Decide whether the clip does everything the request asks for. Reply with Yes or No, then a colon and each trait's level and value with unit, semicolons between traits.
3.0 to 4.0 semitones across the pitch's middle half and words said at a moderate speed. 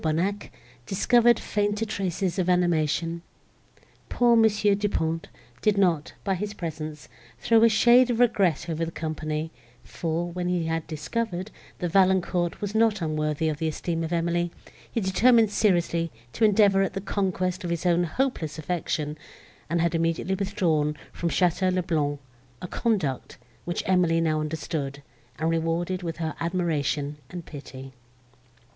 Yes: average, 3.6 semitones; average, 150 wpm